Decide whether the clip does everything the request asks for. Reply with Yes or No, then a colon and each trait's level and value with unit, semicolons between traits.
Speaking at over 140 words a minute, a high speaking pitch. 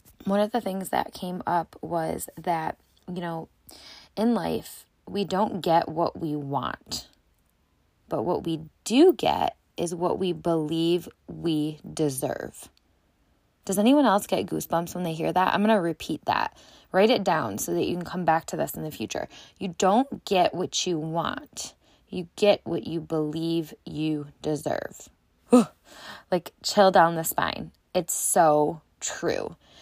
No: average, 160 wpm; medium, 170 Hz